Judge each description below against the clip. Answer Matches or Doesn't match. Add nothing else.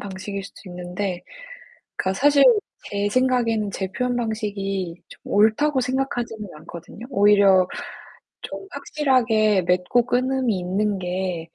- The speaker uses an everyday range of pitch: Matches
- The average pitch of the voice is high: Matches